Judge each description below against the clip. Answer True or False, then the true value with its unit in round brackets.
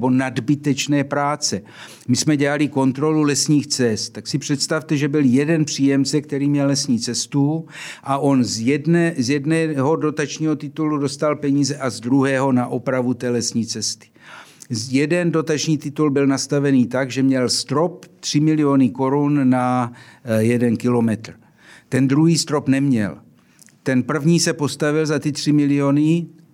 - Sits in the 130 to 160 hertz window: True (140 Hz)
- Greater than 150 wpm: False (145 wpm)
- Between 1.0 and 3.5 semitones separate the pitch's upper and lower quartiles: True (2.8 semitones)